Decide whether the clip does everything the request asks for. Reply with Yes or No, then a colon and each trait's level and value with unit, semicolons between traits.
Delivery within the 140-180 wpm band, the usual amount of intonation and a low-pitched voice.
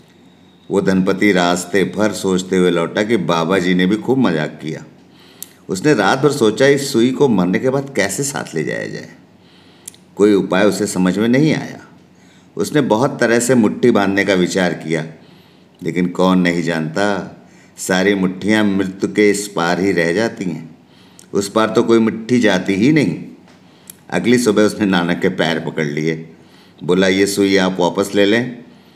Yes: average, 170 wpm; average, 3.9 semitones; low, 100 Hz